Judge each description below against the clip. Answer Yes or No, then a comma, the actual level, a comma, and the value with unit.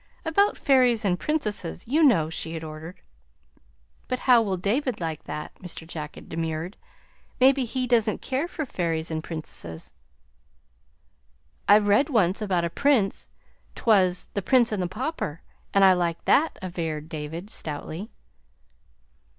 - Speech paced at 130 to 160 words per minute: Yes, average, 150 wpm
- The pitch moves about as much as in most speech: No, wide, 7.3 semitones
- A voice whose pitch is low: No, high, 195 Hz